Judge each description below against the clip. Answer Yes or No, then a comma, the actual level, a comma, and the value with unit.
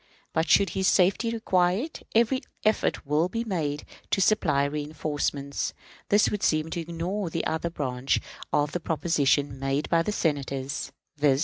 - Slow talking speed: No, average, 155 wpm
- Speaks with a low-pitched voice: No, medium, 160 Hz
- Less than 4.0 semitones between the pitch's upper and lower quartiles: No, average, 4.7 semitones